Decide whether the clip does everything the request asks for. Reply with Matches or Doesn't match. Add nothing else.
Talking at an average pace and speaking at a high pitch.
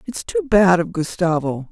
Doesn't match